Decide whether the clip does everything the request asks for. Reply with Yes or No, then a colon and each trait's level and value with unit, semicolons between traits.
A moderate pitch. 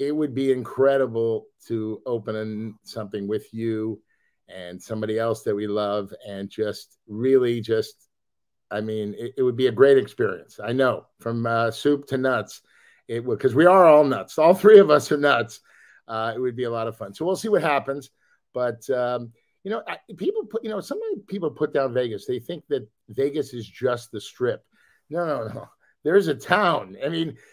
No: low, 125 Hz